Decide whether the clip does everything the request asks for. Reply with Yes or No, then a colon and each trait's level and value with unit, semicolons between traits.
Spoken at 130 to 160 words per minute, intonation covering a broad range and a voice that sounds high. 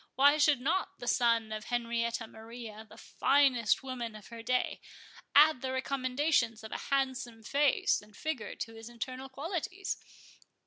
No: average, 150 wpm; average, 3.3 semitones; high, 245 Hz